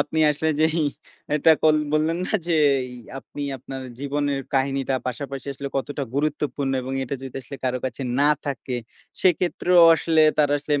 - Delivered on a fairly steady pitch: Yes, narrow, 2.3 semitones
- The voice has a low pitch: No, medium, 145 Hz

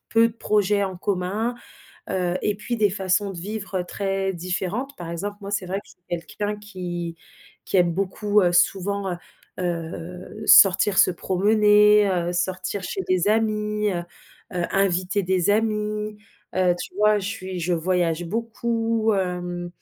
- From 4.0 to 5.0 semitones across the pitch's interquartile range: No, average, 2.8 semitones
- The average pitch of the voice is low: No, high, 195 Hz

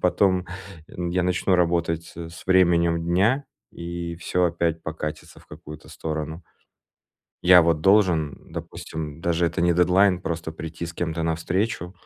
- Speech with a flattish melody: Yes, narrow, 1.6 semitones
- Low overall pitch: Yes, very low, 85 Hz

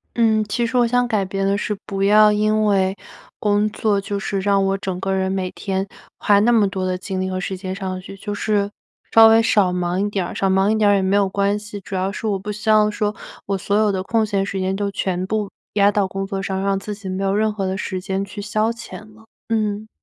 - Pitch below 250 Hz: Yes, high, 200 Hz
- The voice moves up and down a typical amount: No, narrow, 1.7 semitones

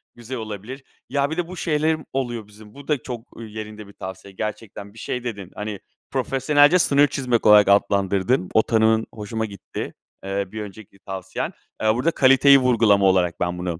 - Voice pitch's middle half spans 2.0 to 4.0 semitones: No, average, 4.7 semitones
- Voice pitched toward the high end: No, low, 110 Hz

